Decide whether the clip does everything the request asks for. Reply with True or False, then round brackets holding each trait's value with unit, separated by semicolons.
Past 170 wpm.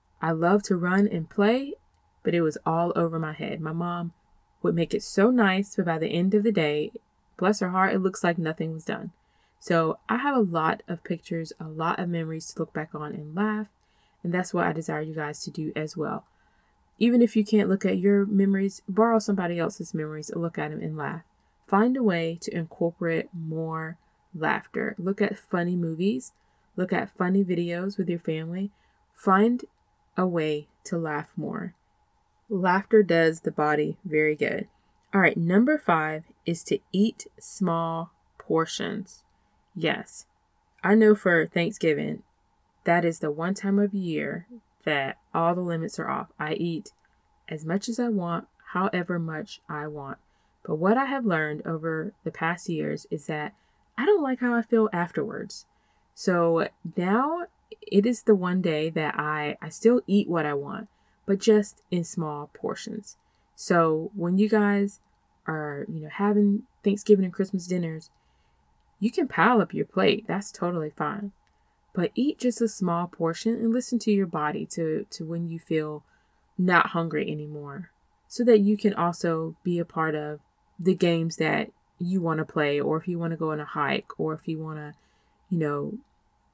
True (180 wpm)